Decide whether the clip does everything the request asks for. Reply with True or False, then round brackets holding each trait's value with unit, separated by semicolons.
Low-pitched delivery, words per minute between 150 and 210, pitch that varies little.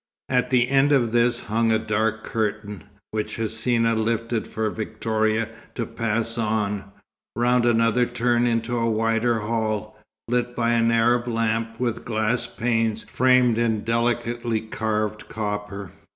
False (115 Hz; 135 wpm; 1.5 semitones)